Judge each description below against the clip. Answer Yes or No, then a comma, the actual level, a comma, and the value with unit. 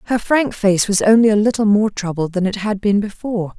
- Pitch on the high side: Yes, high, 205 Hz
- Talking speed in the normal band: No, fast, 235 wpm